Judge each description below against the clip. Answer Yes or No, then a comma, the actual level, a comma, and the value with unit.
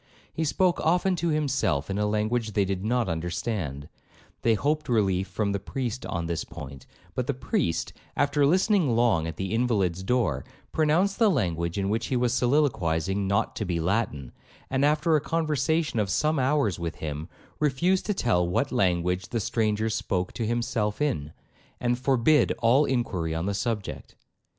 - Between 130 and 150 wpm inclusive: No, average, 170 wpm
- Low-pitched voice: Yes, low, 110 Hz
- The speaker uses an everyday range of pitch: No, wide, 7.5 semitones